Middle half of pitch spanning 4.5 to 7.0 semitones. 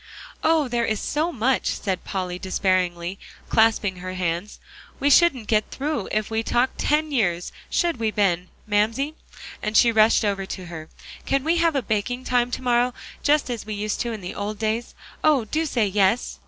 Yes: average, 4.8 semitones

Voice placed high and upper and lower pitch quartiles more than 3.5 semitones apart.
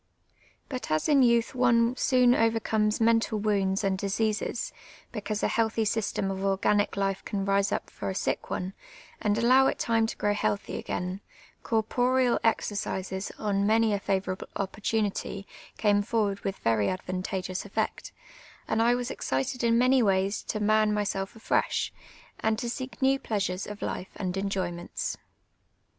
No: high, 210 Hz; average, 2.7 semitones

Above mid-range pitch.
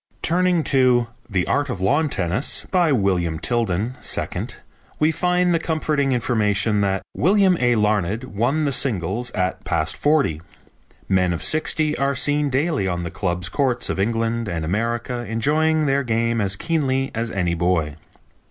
No: low, 120 Hz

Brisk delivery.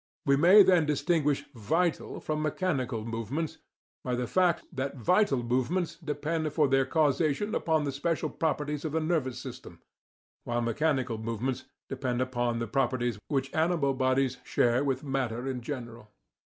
No: average, 155 wpm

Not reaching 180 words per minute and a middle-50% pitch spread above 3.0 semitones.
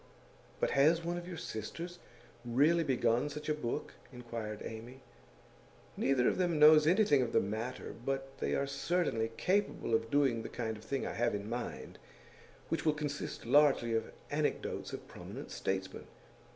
Yes: average, 165 wpm; average, 4.9 semitones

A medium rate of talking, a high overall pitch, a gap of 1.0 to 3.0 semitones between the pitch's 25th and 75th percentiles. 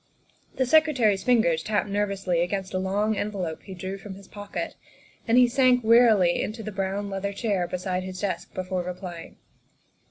Yes: average, 165 wpm; high, 200 Hz; average, 2.7 semitones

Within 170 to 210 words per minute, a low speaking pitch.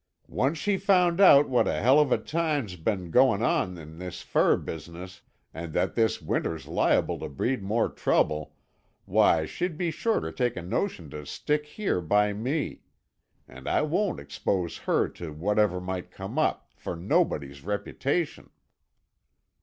No: average, 160 wpm; low, 105 Hz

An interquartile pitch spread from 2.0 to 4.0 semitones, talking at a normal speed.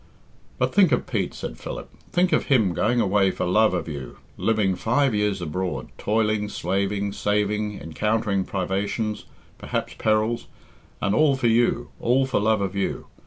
Yes: narrow, 2.6 semitones; average, 160 wpm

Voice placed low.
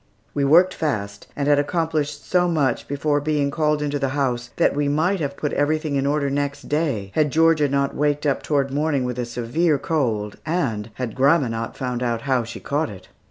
No: medium, 145 Hz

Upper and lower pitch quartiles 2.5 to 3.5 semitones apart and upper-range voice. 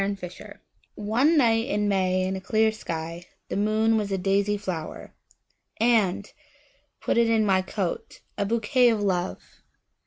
Yes: average, 2.9 semitones; high, 205 Hz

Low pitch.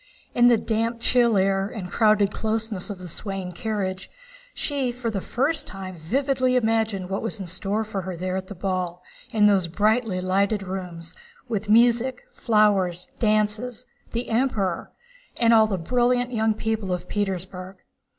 No: high, 210 Hz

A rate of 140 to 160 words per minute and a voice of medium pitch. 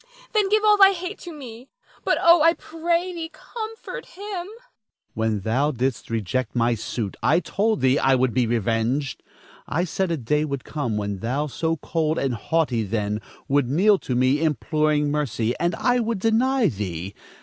No: average, 180 wpm; medium, 150 Hz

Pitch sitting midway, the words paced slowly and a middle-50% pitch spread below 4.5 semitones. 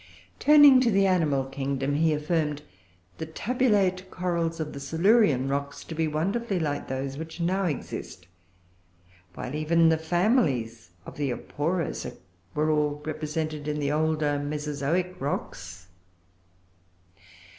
Yes: medium, 155 Hz; slow, 130 wpm; average, 3.8 semitones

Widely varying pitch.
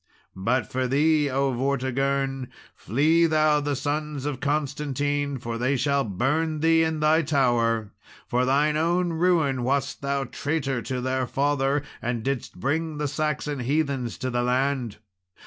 No: average, 2.8 semitones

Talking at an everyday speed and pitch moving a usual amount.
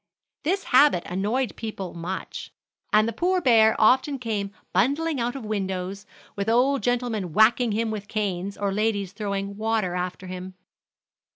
Yes: average, 150 wpm; average, 4.0 semitones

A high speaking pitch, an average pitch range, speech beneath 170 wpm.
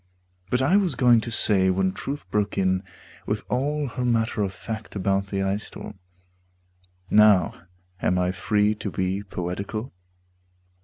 No: low, 105 Hz; average, 3.8 semitones; average, 150 wpm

